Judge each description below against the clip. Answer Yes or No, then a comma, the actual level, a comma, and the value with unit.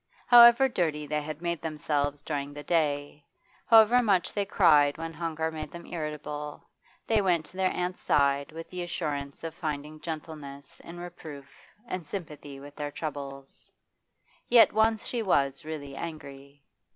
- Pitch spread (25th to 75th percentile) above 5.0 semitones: No, average, 3.4 semitones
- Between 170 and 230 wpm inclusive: No, average, 150 wpm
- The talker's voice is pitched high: No, medium, 155 Hz